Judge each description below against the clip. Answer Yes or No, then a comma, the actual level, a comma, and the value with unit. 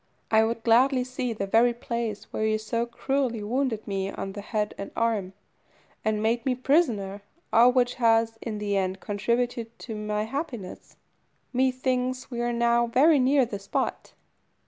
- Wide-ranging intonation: No, average, 2.9 semitones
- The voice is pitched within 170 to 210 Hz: No, high, 230 Hz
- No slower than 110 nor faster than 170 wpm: Yes, average, 165 wpm